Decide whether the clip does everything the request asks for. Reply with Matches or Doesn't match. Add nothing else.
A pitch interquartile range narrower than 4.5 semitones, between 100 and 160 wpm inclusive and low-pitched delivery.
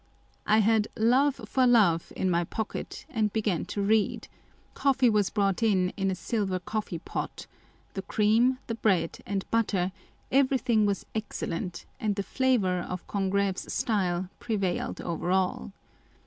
Doesn't match